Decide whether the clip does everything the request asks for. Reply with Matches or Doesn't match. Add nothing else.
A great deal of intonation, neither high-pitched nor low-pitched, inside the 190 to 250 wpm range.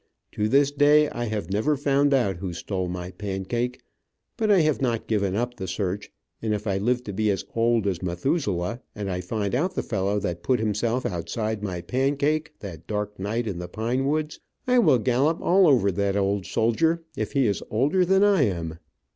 Doesn't match